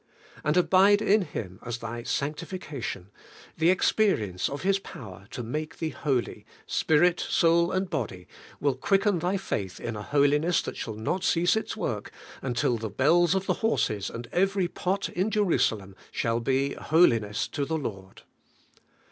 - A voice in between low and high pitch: Yes, medium, 150 Hz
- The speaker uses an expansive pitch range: Yes, wide, 8.0 semitones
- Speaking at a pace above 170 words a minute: No, average, 165 wpm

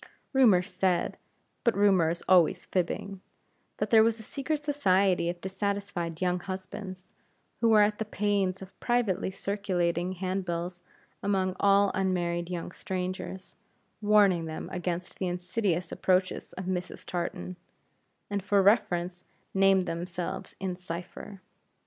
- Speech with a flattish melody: Yes, narrow, 2.1 semitones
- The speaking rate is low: Yes, slow, 130 wpm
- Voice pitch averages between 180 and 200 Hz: Yes, medium, 185 Hz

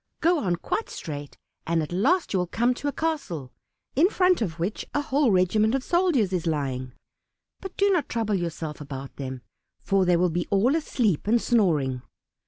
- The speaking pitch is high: Yes, high, 195 Hz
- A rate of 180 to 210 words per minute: Yes, average, 190 wpm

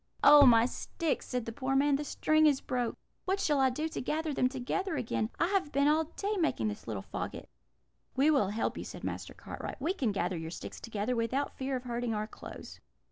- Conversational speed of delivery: No, fast, 220 wpm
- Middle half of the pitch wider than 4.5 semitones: Yes, average, 5.0 semitones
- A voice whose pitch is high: Yes, very high, 265 Hz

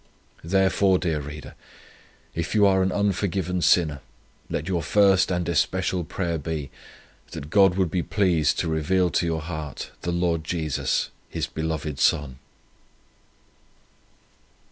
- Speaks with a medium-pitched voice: No, very low, 85 Hz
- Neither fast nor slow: No, slow, 130 wpm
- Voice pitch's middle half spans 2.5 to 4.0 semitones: Yes, average, 3.0 semitones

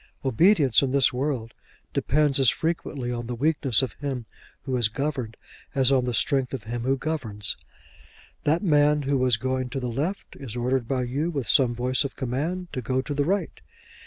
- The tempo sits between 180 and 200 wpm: Yes, average, 190 wpm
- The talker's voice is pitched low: Yes, low, 130 Hz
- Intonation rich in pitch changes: No, average, 3.0 semitones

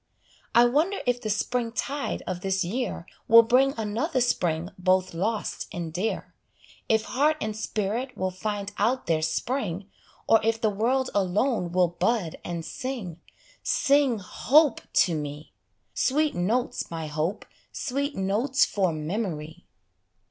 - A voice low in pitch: No, high, 215 Hz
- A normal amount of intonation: No, wide, 5.8 semitones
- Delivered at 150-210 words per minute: No, average, 140 wpm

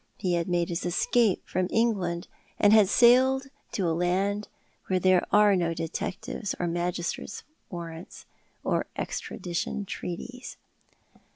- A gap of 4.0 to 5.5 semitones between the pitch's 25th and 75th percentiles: No, average, 3.3 semitones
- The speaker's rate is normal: No, slow, 125 wpm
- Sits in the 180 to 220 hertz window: Yes, medium, 185 Hz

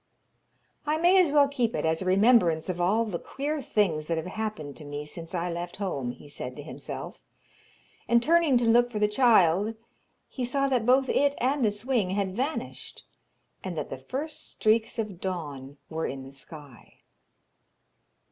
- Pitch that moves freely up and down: Yes, wide, 7.5 semitones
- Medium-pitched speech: No, high, 205 Hz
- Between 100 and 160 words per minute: No, average, 180 wpm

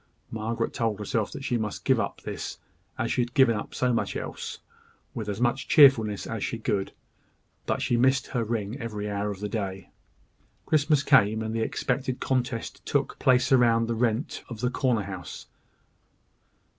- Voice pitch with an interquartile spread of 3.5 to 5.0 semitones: No, average, 2.9 semitones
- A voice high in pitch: No, low, 115 Hz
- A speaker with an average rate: Yes, average, 175 wpm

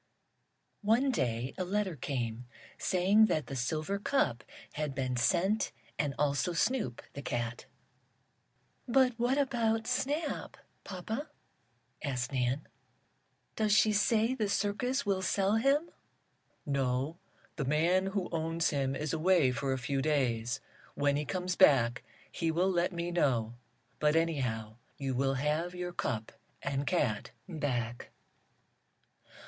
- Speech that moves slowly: Yes, slow, 130 wpm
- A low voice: No, medium, 160 Hz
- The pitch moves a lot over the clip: Yes, wide, 7.0 semitones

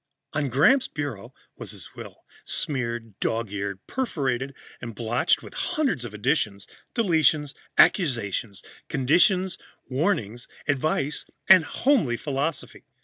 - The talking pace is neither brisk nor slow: No, slow, 110 wpm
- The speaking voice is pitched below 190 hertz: Yes, low, 135 Hz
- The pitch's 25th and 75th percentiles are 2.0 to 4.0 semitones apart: No, wide, 5.6 semitones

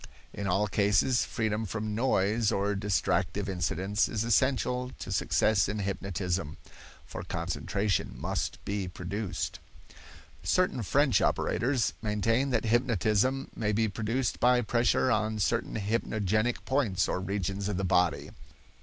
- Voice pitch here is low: Yes, low, 105 Hz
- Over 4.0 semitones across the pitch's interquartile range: No, average, 3.1 semitones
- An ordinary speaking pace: No, slow, 125 wpm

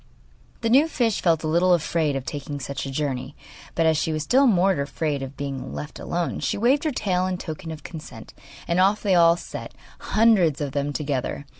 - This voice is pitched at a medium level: Yes, medium, 160 Hz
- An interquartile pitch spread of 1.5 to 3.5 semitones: No, average, 4.6 semitones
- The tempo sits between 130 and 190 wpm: No, fast, 205 wpm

